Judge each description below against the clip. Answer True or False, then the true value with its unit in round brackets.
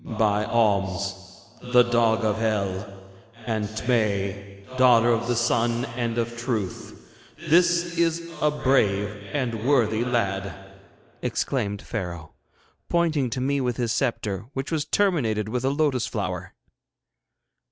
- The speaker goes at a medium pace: False (125 wpm)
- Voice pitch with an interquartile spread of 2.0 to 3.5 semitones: False (4.1 semitones)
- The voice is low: True (115 Hz)